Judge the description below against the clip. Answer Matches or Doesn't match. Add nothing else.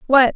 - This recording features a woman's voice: Matches